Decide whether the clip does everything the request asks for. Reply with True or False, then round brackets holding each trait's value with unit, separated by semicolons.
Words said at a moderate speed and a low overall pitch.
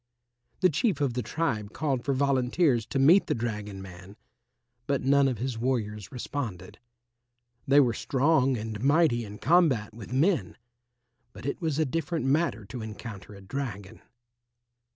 True (150 wpm; 130 Hz)